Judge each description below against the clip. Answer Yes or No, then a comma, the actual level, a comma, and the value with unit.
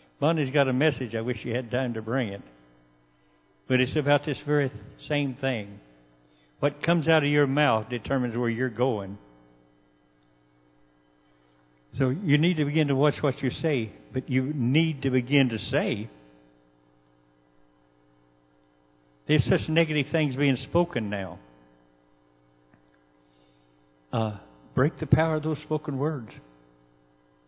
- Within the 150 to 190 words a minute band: No, average, 140 wpm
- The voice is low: Yes, low, 110 Hz